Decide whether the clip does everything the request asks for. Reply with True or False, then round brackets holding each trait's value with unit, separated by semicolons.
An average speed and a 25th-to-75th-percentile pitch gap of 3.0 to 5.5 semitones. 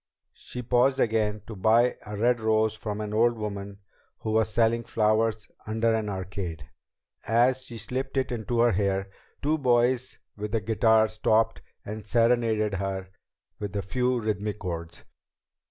False (155 wpm; 2.4 semitones)